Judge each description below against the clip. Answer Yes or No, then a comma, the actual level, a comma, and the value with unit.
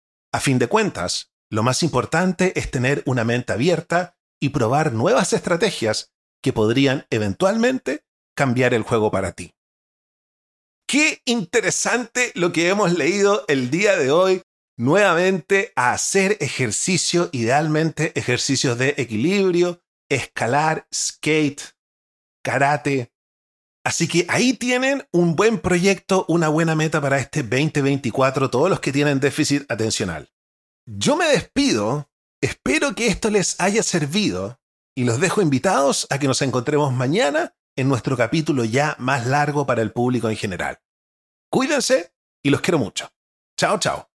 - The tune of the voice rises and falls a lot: Yes, wide, 6.8 semitones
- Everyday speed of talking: Yes, average, 135 wpm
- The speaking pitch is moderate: Yes, medium, 145 Hz